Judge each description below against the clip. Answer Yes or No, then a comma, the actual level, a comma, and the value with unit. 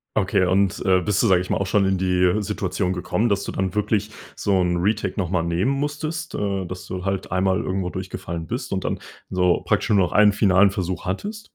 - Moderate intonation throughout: No, narrow, 2.1 semitones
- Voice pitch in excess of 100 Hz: No, very low, 95 Hz